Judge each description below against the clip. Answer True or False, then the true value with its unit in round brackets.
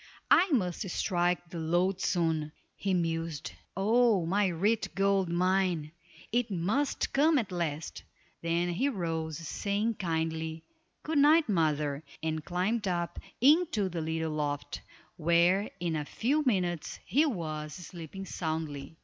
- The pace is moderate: False (130 wpm)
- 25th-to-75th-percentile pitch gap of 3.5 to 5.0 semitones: True (4.0 semitones)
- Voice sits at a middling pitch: True (175 Hz)